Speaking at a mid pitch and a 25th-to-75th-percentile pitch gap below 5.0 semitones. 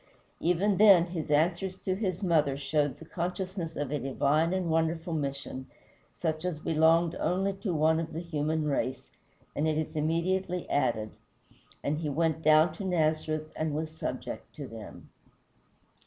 Yes: medium, 160 Hz; narrow, 2.6 semitones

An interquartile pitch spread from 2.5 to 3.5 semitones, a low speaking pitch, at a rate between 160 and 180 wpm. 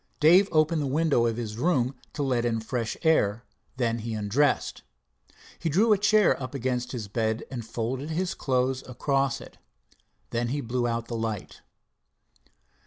No: average, 4.2 semitones; low, 125 Hz; average, 165 wpm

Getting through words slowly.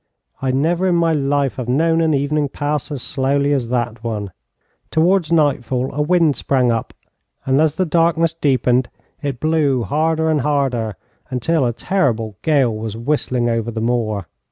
No: average, 165 wpm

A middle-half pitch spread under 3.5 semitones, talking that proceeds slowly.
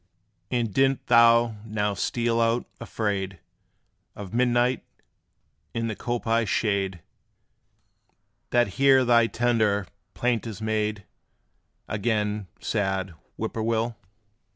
Yes: narrow, 2.4 semitones; slow, 105 wpm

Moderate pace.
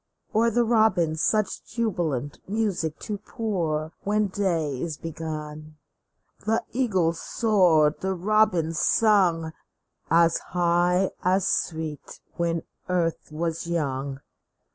No: slow, 105 wpm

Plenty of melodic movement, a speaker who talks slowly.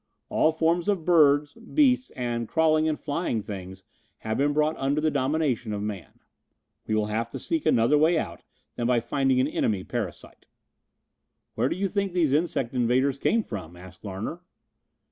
No: wide, 6.4 semitones; average, 170 wpm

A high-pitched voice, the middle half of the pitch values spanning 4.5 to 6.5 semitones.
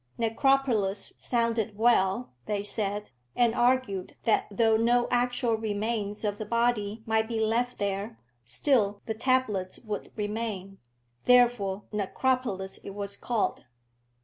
No: high, 220 Hz; average, 3.0 semitones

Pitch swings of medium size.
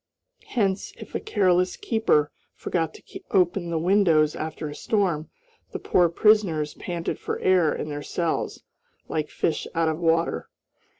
Yes: average, 3.4 semitones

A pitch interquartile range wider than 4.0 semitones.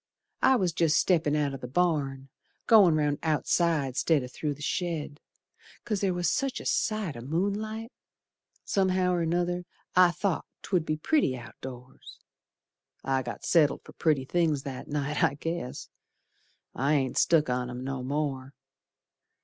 Yes: average, 4.6 semitones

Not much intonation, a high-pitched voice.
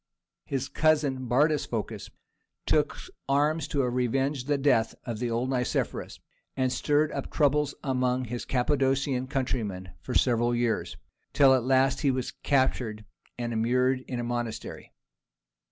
No: narrow, 2.3 semitones; low, 130 Hz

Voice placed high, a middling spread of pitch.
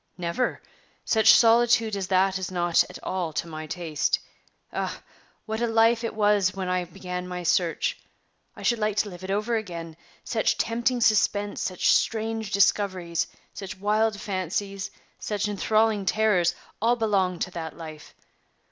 Yes: high, 200 Hz; average, 3.4 semitones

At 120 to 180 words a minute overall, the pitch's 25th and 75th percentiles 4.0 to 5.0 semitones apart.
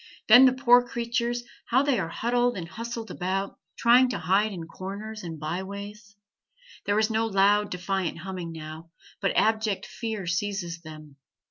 Yes: average, 160 wpm; average, 4.5 semitones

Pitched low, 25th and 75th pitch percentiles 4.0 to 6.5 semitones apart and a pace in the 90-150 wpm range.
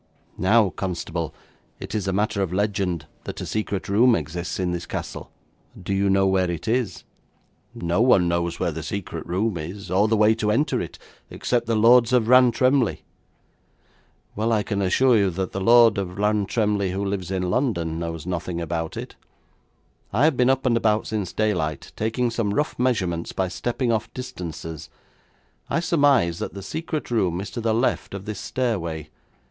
No: low, 100 Hz; average, 4.5 semitones; average, 180 wpm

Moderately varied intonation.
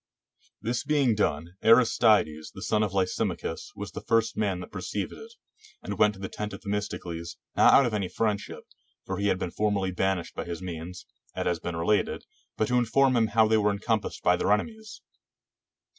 Yes: average, 3.7 semitones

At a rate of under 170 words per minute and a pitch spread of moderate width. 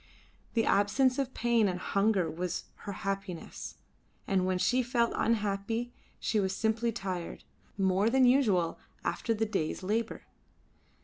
Yes: slow, 135 wpm; average, 3.6 semitones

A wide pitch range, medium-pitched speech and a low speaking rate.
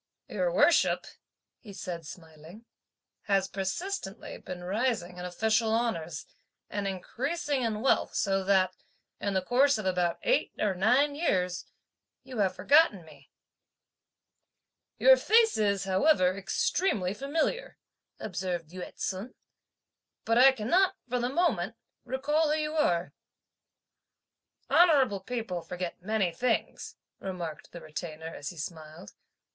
No: wide, 6.7 semitones; high, 200 Hz; slow, 125 wpm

